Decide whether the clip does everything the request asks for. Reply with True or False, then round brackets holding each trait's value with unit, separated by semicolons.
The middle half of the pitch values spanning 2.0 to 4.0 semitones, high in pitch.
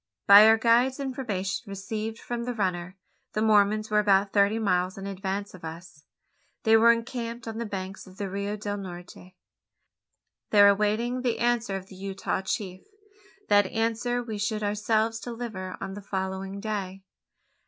True (2.7 semitones; 205 Hz)